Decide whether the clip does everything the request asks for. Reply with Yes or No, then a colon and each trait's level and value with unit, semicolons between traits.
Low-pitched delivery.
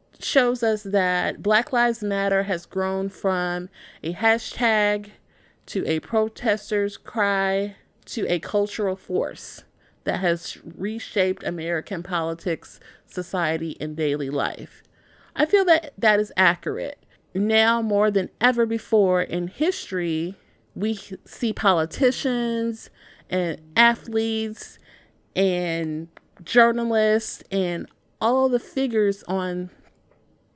No: high, 195 Hz